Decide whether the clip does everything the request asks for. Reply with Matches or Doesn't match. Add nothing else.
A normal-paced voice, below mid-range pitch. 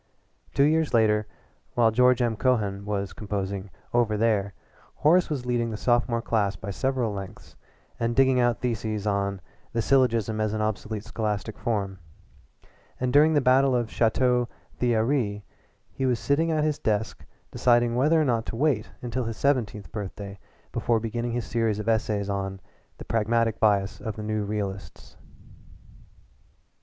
Matches